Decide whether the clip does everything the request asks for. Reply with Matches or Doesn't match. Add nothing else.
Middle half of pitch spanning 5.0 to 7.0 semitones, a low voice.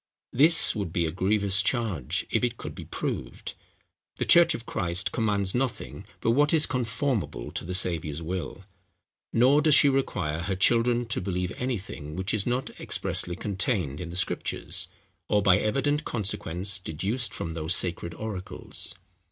Matches